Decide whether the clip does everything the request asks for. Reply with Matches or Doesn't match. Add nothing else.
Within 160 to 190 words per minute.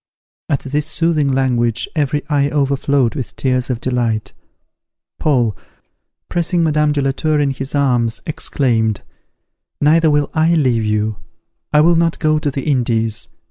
Doesn't match